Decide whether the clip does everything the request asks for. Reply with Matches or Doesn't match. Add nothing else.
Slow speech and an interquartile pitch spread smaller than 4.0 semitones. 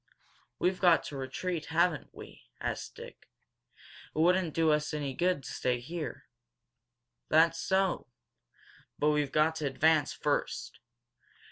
Matches